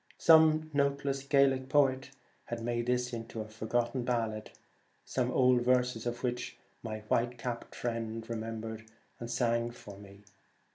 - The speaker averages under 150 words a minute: Yes, average, 140 wpm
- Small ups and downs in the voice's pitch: Yes, narrow, 2.3 semitones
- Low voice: Yes, low, 120 Hz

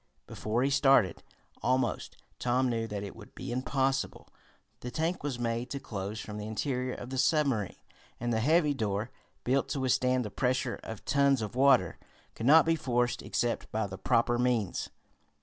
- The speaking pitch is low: Yes, low, 125 Hz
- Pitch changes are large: No, average, 3.4 semitones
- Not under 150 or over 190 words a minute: Yes, average, 175 wpm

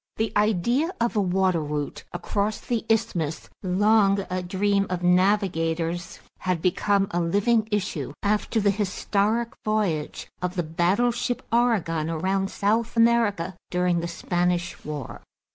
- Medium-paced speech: No, slow, 130 wpm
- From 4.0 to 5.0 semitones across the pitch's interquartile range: No, average, 3.6 semitones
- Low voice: No, high, 195 Hz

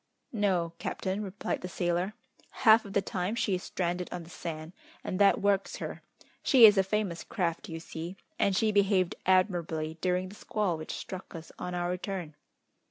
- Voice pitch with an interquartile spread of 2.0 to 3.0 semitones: Yes, narrow, 2.6 semitones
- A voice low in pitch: No, medium, 185 Hz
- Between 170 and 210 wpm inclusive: Yes, average, 180 wpm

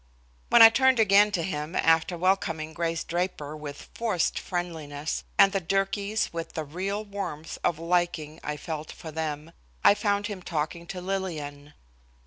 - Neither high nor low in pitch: Yes, medium, 170 Hz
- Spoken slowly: No, average, 155 wpm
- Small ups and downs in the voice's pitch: No, average, 4.0 semitones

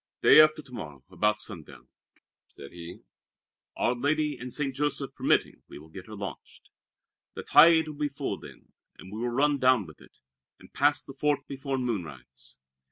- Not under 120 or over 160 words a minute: No, average, 175 wpm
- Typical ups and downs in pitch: No, wide, 6.7 semitones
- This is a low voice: Yes, low, 130 Hz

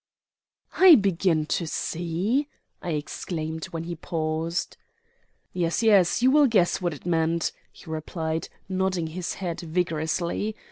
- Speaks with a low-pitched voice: No, medium, 170 Hz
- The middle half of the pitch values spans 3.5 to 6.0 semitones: No, average, 2.9 semitones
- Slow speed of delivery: Yes, slow, 130 wpm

